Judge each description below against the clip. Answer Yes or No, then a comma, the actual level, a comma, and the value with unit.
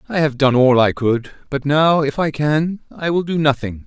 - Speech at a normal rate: No, fast, 235 wpm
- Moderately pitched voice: Yes, medium, 145 Hz